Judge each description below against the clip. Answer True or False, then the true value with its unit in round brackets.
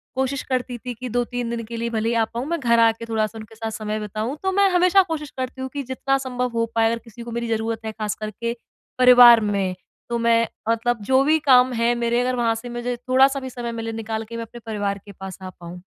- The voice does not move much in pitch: True (2.1 semitones)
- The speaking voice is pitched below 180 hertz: False (235 Hz)